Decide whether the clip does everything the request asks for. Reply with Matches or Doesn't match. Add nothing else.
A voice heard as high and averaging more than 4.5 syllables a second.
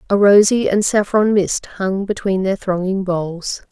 Doesn't match